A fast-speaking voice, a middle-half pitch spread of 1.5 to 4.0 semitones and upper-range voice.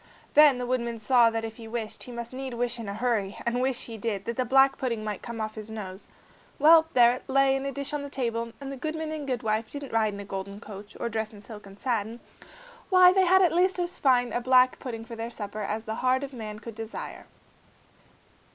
Yes: fast, 245 wpm; average, 3.5 semitones; high, 235 Hz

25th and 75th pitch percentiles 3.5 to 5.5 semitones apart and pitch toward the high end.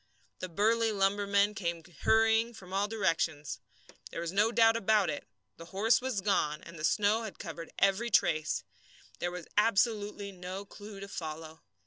Yes: average, 4.1 semitones; high, 200 Hz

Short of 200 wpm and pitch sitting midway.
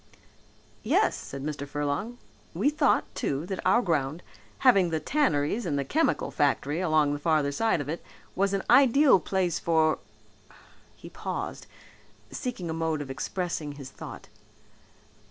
Yes: average, 150 wpm; medium, 160 Hz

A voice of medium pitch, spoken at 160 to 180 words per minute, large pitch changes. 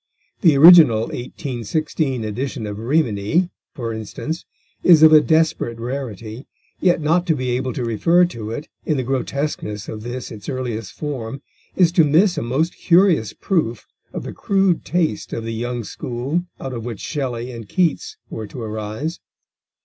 No: low, 130 Hz; average, 165 wpm; wide, 5.8 semitones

